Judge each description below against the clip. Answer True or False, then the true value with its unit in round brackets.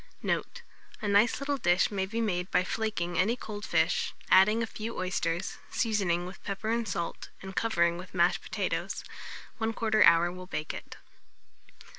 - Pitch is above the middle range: True (195 Hz)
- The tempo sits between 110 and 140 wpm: False (160 wpm)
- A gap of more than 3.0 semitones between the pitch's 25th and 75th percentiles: True (4.0 semitones)